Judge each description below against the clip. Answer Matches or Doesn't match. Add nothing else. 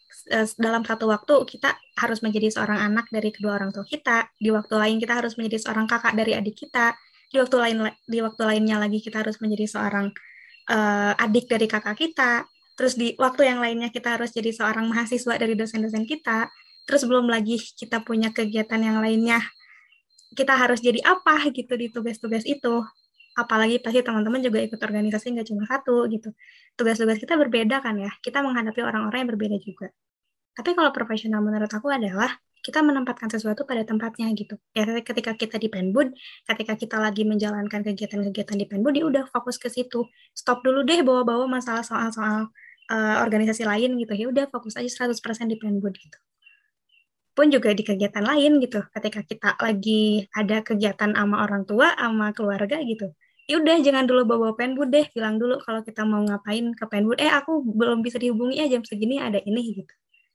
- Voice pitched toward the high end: Matches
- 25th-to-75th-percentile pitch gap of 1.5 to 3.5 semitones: Matches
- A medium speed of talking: Doesn't match